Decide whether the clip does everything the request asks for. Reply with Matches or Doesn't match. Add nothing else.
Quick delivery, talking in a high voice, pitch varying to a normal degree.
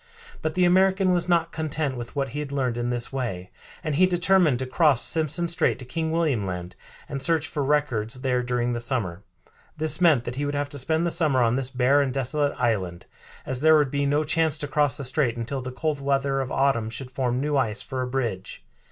Doesn't match